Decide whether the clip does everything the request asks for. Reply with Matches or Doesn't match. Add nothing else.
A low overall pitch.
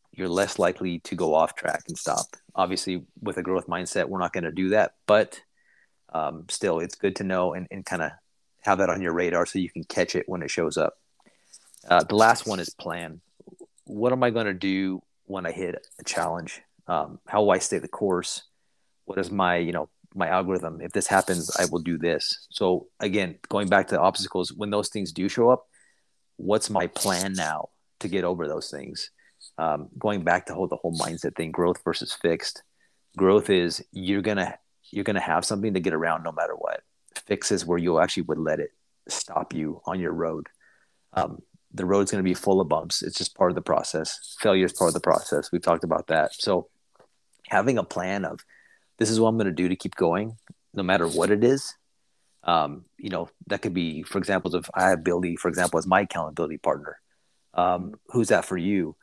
Matches